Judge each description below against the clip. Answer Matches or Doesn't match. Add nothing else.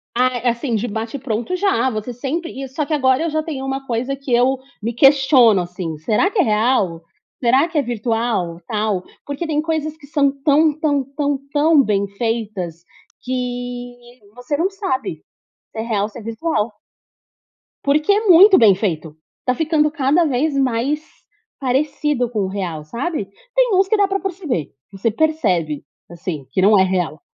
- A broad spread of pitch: Matches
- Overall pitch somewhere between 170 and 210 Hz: Doesn't match